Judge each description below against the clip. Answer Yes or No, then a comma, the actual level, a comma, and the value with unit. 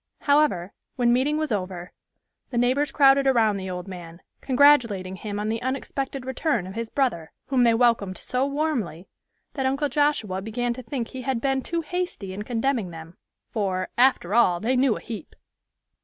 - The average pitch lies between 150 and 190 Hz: No, high, 240 Hz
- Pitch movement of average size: No, wide, 5.7 semitones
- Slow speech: No, average, 175 wpm